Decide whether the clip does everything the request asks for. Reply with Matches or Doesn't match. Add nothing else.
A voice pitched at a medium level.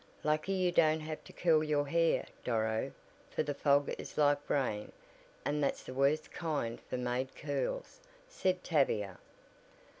Matches